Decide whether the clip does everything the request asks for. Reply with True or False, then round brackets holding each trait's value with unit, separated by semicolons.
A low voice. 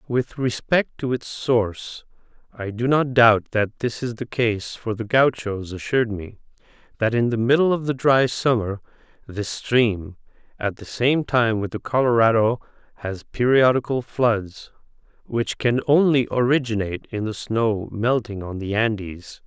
True (115 Hz)